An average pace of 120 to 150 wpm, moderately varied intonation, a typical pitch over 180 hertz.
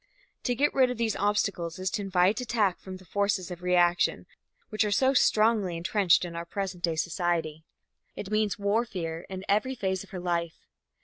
No: average, 185 wpm; average, 3.5 semitones; high, 190 Hz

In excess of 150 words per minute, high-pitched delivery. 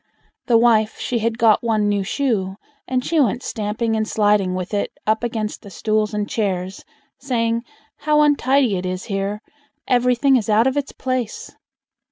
Yes: average, 170 wpm; high, 220 Hz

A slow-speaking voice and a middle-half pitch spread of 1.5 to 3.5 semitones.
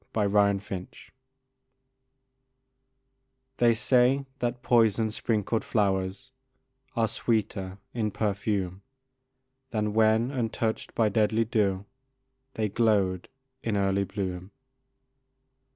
Yes: slow, 90 wpm; narrow, 2.5 semitones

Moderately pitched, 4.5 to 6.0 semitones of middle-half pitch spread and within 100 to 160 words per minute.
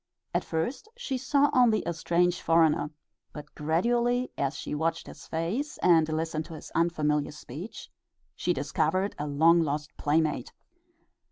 Yes: medium, 165 Hz; wide, 5.4 semitones; average, 145 wpm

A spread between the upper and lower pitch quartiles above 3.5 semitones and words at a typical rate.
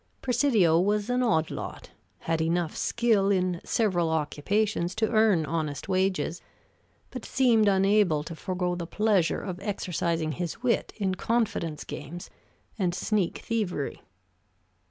No: average, 4.3 semitones; slow, 130 wpm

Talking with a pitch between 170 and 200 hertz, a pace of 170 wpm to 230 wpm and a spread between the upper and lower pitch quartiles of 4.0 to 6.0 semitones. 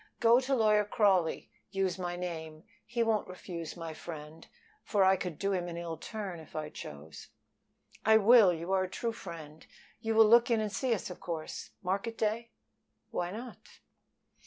Yes: high, 190 Hz; average, 180 wpm; average, 4.7 semitones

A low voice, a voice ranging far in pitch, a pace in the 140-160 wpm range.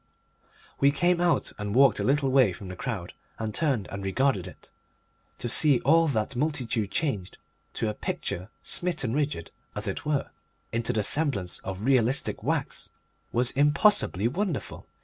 Yes: low, 125 Hz; wide, 5.8 semitones; average, 155 wpm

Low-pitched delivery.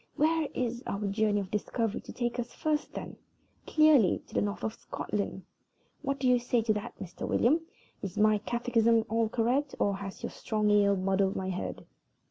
No: high, 220 Hz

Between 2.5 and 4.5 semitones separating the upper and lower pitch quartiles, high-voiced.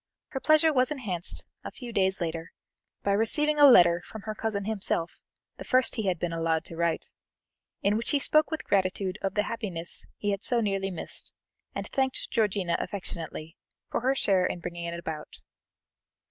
No: wide, 5.4 semitones; high, 200 Hz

